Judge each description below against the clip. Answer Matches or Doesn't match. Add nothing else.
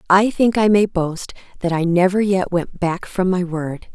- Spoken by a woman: Matches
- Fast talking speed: Matches